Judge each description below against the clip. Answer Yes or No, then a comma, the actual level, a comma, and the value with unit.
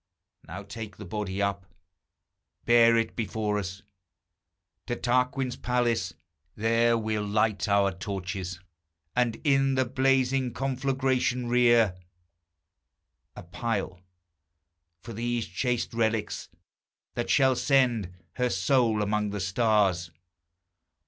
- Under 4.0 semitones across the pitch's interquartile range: Yes, average, 3.5 semitones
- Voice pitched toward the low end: Yes, low, 115 Hz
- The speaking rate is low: Yes, slow, 105 wpm